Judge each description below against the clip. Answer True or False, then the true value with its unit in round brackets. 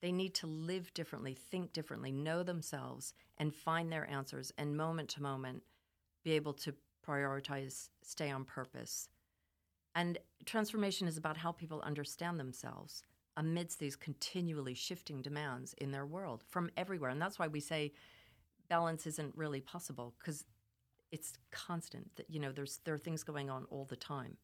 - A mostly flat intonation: False (3.7 semitones)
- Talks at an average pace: True (160 wpm)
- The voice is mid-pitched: True (150 Hz)